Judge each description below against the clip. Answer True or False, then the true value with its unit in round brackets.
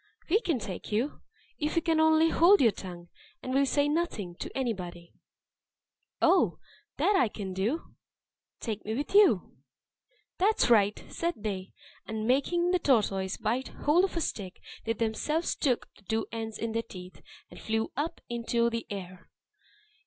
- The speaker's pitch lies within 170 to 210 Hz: False (230 Hz)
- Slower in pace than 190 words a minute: True (160 wpm)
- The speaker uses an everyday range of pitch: False (7.4 semitones)